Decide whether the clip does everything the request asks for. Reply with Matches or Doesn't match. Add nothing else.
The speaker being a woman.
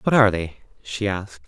Doesn't match